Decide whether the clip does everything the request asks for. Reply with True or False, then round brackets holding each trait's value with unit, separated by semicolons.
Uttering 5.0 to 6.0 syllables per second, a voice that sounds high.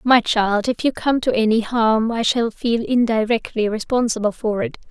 False (4.5 syllables/s; 225 Hz)